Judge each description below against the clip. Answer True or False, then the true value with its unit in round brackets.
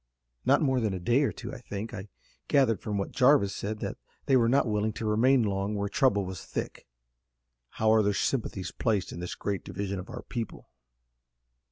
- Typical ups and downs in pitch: True (3.7 semitones)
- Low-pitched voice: True (110 Hz)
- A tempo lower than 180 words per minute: False (200 wpm)